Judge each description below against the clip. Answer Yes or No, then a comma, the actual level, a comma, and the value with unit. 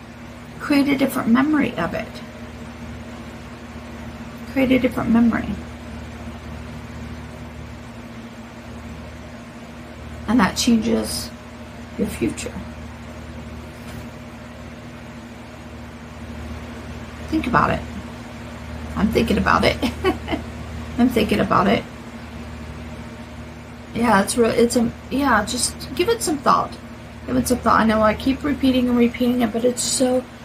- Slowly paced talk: Yes, slow, 100 wpm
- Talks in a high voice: Yes, high, 215 Hz